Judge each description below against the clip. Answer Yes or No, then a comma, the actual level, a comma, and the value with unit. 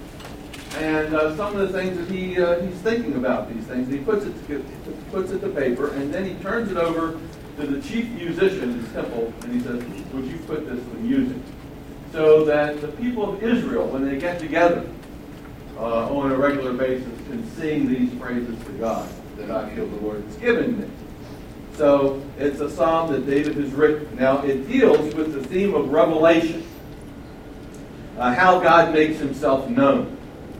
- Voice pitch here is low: No, medium, 155 Hz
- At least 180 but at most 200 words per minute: Yes, average, 190 wpm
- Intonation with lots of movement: No, average, 5.0 semitones